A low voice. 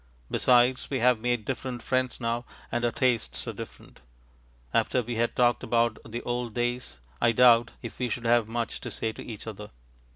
Yes: low, 120 Hz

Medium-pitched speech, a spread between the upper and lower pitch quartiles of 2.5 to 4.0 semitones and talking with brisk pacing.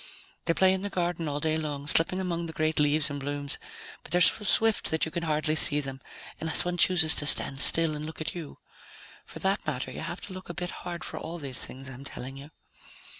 Yes: medium, 160 Hz; average, 3.3 semitones; fast, 235 wpm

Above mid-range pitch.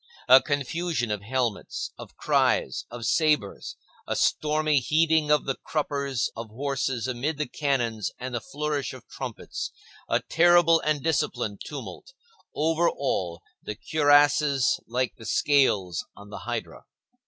No: low, 135 Hz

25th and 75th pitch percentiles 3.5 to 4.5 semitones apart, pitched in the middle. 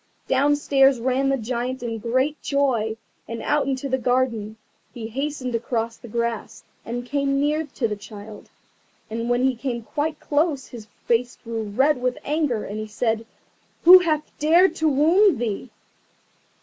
No: average, 3.9 semitones; very high, 255 Hz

